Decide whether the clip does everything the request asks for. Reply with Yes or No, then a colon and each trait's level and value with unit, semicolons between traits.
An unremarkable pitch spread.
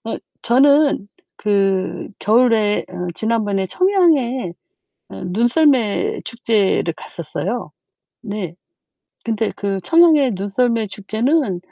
Yes: average, 4.9 semitones